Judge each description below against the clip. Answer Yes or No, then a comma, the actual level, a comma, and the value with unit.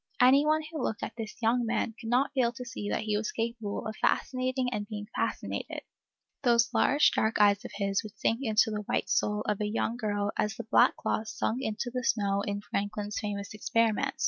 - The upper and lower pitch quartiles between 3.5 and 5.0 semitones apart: No, average, 2.8 semitones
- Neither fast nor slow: No, fast, 210 wpm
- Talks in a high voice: Yes, high, 220 Hz